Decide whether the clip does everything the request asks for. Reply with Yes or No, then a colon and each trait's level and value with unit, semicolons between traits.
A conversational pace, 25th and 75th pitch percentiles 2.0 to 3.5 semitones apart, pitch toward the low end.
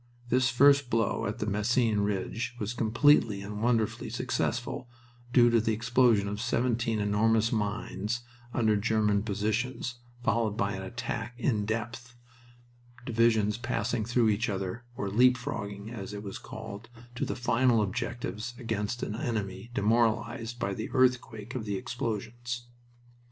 Yes: average, 145 wpm; narrow, 2.5 semitones; low, 115 Hz